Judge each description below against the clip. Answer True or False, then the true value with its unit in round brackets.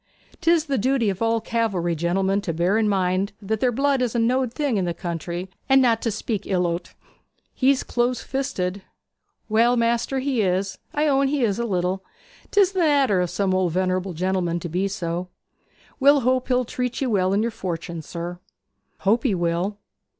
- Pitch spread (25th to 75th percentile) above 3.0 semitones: True (5.6 semitones)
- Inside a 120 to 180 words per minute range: False (190 wpm)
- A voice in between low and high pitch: False (210 Hz)